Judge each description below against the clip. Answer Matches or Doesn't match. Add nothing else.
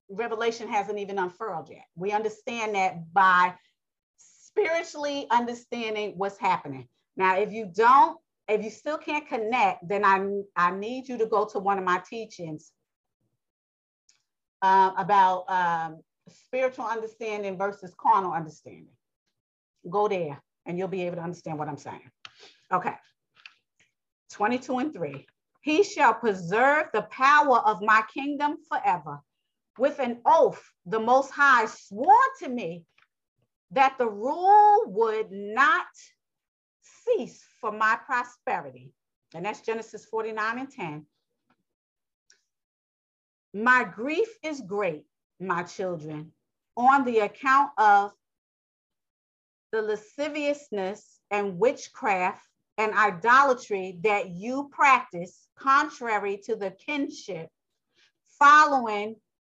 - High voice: Matches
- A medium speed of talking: Doesn't match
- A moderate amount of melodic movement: Doesn't match